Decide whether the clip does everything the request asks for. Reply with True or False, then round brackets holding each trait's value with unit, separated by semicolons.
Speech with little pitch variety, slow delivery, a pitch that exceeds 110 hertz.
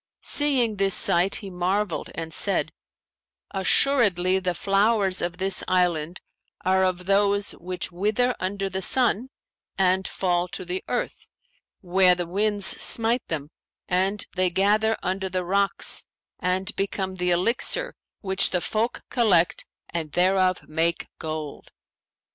True (2.2 semitones; 130 wpm; 190 Hz)